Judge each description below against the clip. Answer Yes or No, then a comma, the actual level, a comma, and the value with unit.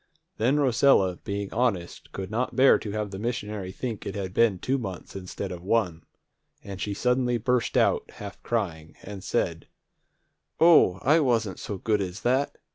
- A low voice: Yes, low, 105 Hz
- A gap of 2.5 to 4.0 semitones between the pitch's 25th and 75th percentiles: No, average, 4.5 semitones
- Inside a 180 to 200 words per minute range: No, average, 170 wpm